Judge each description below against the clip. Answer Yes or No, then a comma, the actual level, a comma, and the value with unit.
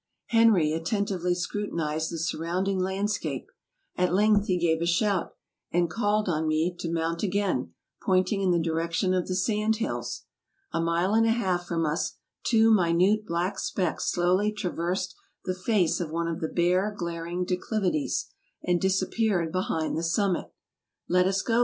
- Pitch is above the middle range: No, medium, 180 Hz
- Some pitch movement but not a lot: Yes, average, 3.2 semitones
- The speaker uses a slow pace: No, average, 160 wpm